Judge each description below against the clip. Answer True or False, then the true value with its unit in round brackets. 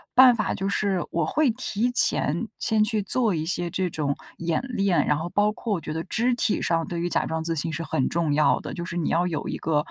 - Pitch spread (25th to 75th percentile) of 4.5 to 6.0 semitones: True (4.8 semitones)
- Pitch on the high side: False (175 Hz)